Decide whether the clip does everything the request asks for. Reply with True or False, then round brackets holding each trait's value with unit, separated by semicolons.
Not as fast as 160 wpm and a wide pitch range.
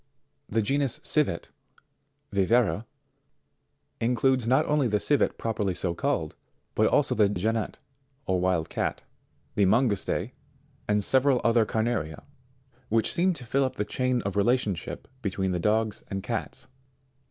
False (140 wpm; 4.2 semitones)